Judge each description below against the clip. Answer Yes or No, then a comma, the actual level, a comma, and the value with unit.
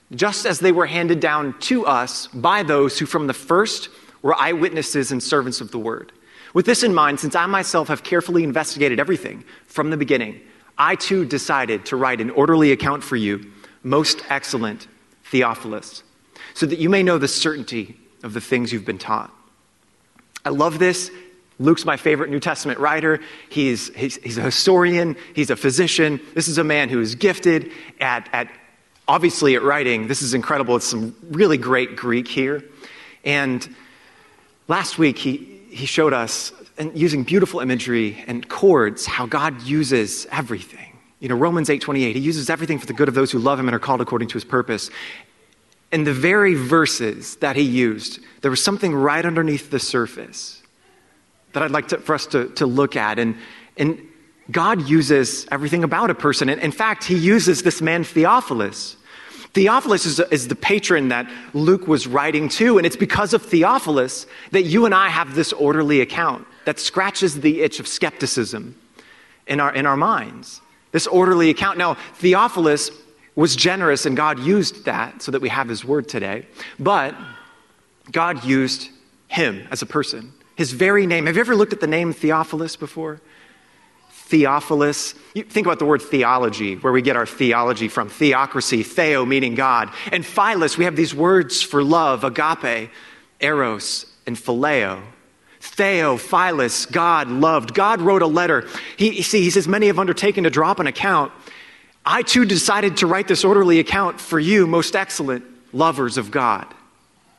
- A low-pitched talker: No, medium, 150 Hz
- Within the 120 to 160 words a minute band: No, average, 175 wpm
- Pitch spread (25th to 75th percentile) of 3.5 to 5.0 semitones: Yes, average, 4.5 semitones